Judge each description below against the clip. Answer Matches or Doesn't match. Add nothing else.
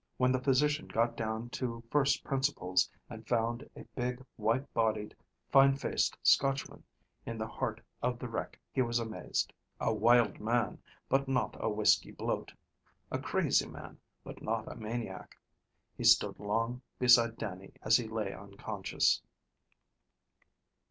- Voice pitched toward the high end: Doesn't match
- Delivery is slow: Doesn't match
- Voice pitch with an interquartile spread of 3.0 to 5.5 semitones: Doesn't match